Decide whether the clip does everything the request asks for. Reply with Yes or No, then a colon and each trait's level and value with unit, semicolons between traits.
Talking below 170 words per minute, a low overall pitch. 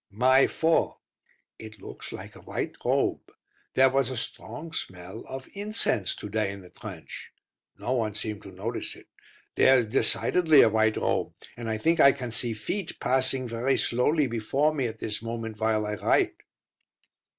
No: average, 175 wpm; low, 115 Hz